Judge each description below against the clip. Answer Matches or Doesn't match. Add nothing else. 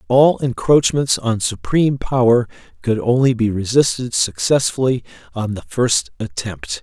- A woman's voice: Doesn't match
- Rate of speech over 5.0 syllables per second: Doesn't match